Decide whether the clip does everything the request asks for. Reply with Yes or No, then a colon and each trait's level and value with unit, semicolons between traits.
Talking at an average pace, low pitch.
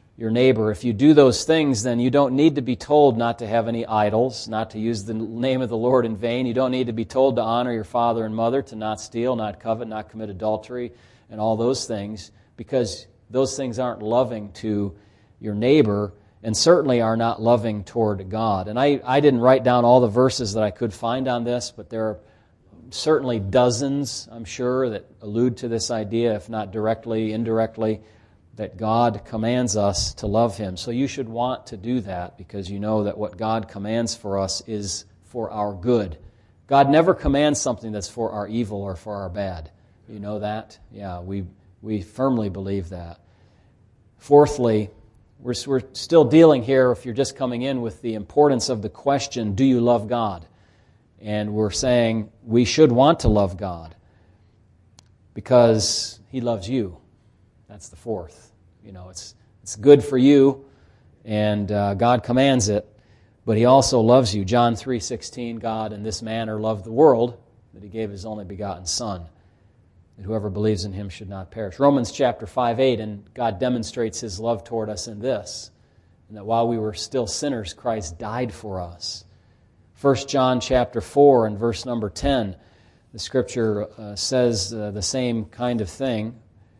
Yes: average, 185 wpm; low, 110 Hz